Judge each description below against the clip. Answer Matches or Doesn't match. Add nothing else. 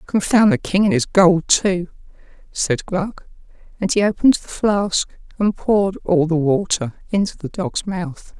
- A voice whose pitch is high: Matches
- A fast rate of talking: Doesn't match